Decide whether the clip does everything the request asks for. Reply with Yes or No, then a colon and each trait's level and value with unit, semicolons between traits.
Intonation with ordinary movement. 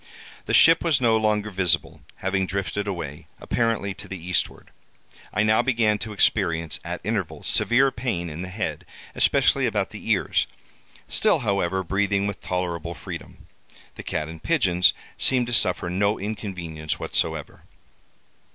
Yes: average, 3.5 semitones